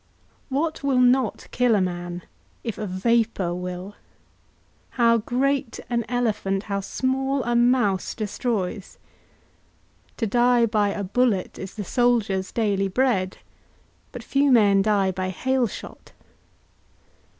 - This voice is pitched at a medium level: No, high, 220 Hz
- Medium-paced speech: No, slow, 125 wpm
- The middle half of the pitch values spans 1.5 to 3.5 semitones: No, average, 4.2 semitones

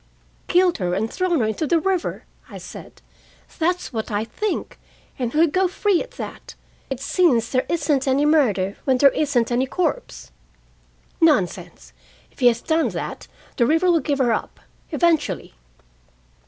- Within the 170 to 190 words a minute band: No, average, 160 wpm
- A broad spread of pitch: Yes, wide, 6.1 semitones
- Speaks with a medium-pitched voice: No, very high, 290 Hz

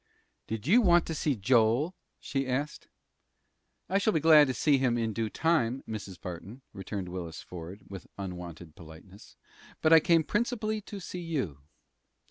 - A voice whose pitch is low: Yes, low, 125 Hz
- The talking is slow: No, average, 160 wpm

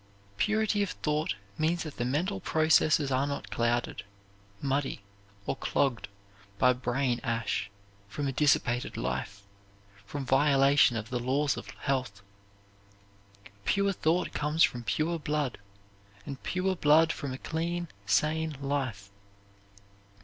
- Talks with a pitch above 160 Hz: No, medium, 140 Hz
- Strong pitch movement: No, average, 4.2 semitones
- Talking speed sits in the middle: No, slow, 125 wpm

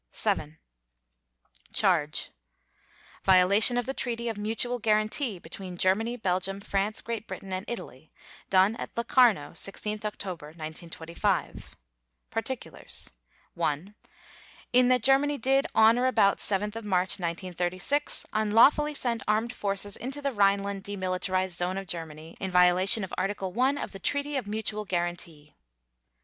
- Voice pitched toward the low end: No, high, 200 Hz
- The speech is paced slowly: Yes, slow, 130 wpm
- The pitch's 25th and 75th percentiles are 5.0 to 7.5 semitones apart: No, average, 4.3 semitones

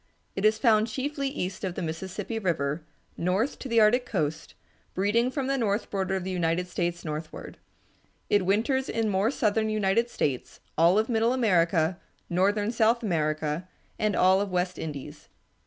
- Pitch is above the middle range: Yes, high, 195 Hz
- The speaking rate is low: No, average, 165 wpm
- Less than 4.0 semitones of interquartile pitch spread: No, average, 4.5 semitones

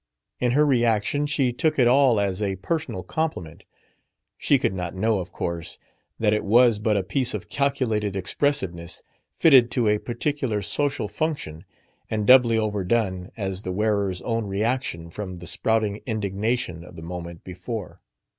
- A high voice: No, low, 105 Hz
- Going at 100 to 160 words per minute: Yes, average, 155 wpm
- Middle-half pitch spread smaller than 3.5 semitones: No, average, 4.8 semitones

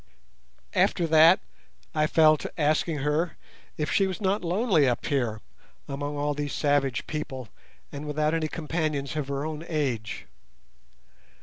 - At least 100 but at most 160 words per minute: Yes, average, 140 wpm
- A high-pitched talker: No, medium, 150 Hz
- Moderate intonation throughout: No, narrow, 2.3 semitones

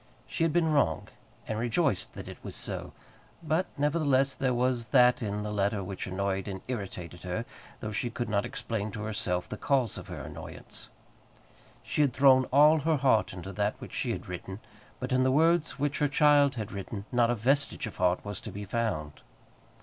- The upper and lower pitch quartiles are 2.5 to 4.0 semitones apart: No, wide, 5.6 semitones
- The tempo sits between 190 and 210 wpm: Yes, average, 195 wpm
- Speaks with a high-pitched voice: No, low, 115 Hz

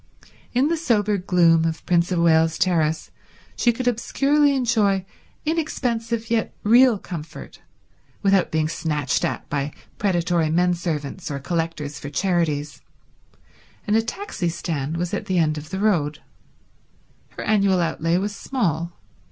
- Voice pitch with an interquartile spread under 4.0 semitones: No, average, 5.3 semitones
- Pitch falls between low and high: Yes, medium, 175 Hz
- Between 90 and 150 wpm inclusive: Yes, average, 140 wpm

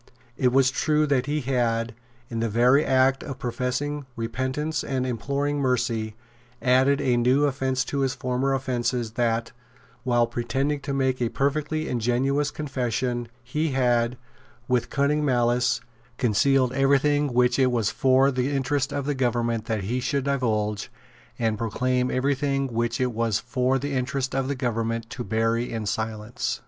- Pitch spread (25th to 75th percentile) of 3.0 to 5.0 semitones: No, narrow, 2.5 semitones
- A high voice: No, low, 125 Hz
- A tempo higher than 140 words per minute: Yes, average, 160 wpm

